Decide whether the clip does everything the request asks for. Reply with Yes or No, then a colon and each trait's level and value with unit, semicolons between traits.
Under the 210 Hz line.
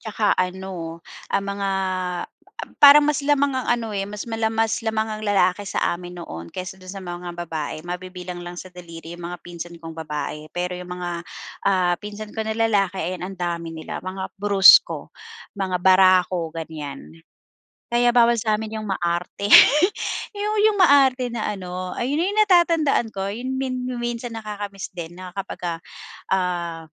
Yes: high, 190 Hz